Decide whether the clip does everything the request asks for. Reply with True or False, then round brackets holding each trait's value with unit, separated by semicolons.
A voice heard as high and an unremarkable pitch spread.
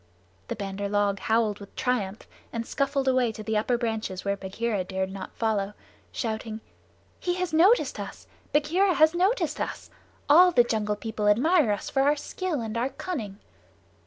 False (230 Hz; 6.3 semitones)